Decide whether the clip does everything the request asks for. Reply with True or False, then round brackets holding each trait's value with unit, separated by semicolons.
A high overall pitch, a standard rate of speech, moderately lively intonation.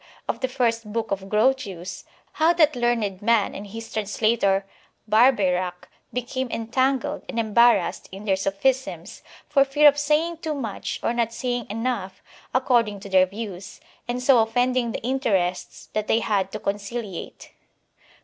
True (230 Hz; 150 wpm; 4.3 semitones)